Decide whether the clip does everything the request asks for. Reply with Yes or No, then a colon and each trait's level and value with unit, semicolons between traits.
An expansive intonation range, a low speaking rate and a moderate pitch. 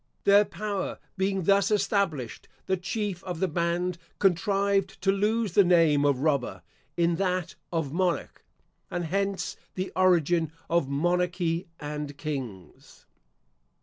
No: average, 3.3 semitones; slow, 125 wpm; medium, 180 Hz